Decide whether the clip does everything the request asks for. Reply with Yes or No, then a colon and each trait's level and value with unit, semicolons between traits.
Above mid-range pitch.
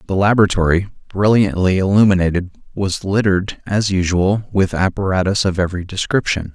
No: very low, 95 Hz